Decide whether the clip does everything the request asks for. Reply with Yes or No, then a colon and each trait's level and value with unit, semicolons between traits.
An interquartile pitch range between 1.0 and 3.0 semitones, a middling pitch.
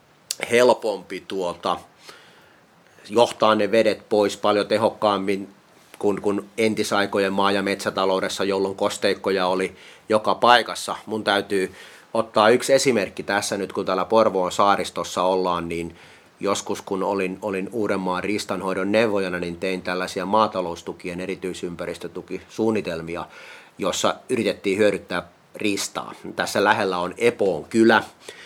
No: narrow, 2.6 semitones; low, 100 Hz